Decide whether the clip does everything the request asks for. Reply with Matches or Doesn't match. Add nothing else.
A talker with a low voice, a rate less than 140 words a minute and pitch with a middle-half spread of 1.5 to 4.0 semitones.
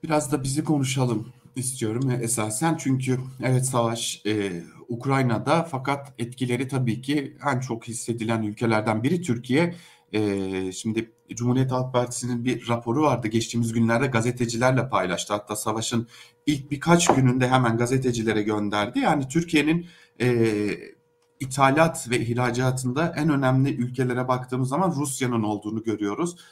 Matches